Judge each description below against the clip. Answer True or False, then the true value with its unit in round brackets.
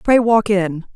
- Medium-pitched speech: False (205 Hz)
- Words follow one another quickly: False (190 wpm)